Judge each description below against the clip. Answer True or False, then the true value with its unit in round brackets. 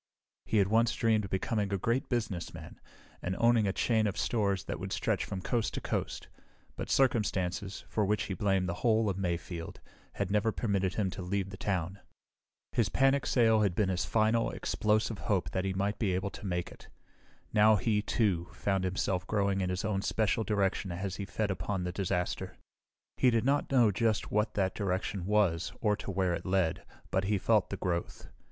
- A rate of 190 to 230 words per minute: True (195 wpm)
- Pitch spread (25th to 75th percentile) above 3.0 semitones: False (2.6 semitones)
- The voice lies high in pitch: False (100 Hz)